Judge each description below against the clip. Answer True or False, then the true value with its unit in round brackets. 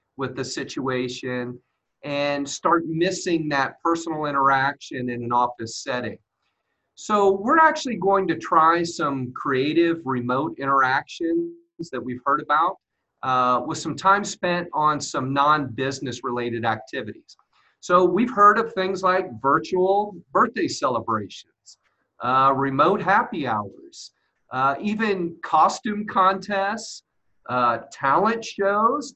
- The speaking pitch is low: False (160 Hz)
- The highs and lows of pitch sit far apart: True (6.8 semitones)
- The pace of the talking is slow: True (120 wpm)